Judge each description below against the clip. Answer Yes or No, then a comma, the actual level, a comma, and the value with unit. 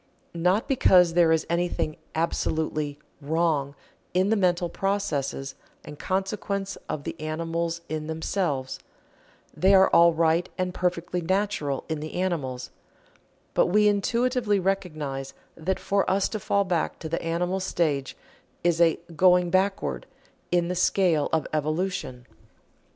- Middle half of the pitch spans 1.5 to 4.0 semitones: Yes, average, 3.4 semitones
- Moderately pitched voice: Yes, medium, 170 Hz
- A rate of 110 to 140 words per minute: Yes, slow, 135 wpm